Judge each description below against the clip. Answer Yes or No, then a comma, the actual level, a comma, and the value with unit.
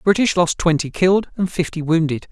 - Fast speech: Yes, fast, 210 wpm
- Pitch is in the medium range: Yes, medium, 170 Hz